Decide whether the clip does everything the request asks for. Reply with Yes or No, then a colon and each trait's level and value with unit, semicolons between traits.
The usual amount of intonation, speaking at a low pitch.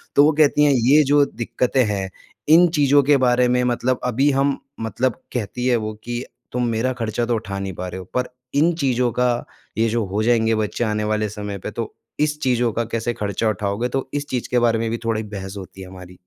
Yes: average, 3.2 semitones; low, 120 Hz